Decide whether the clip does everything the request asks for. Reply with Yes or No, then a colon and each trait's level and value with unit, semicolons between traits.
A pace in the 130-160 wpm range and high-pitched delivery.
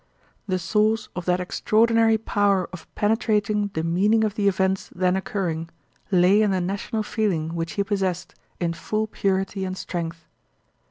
Yes: average, 155 wpm; high, 195 Hz